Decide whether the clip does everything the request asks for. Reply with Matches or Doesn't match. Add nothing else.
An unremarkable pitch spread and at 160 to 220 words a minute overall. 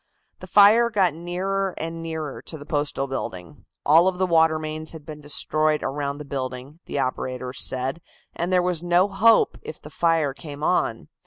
Matches